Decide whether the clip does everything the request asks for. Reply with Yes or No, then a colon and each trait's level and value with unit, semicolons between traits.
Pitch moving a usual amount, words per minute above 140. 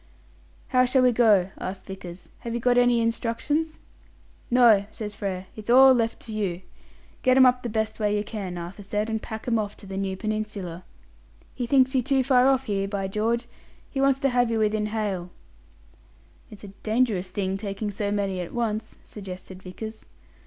Yes: average, 3.7 semitones; average, 180 wpm